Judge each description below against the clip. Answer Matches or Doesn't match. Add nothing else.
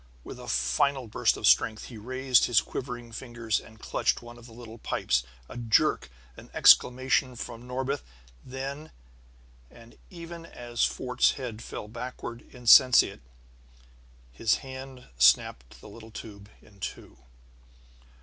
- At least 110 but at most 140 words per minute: Matches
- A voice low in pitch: Matches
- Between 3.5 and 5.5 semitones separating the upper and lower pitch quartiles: Doesn't match